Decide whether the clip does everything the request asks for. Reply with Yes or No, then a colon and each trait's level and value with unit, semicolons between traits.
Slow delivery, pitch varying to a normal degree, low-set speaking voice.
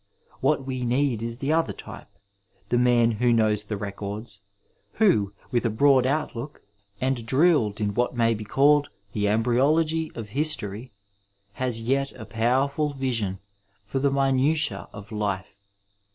No: average, 150 wpm; average, 4.4 semitones; low, 120 Hz